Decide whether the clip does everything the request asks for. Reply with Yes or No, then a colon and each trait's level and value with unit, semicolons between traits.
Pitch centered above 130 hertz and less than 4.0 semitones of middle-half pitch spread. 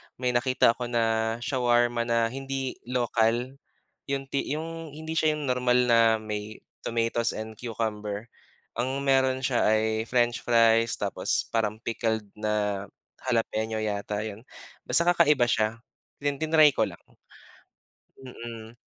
No: low, 120 Hz; average, 2.9 semitones